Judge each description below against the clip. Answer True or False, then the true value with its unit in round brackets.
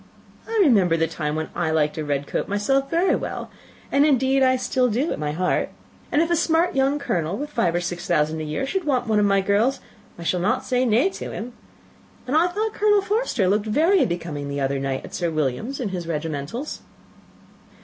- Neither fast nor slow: False (220 wpm)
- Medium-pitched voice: False (210 Hz)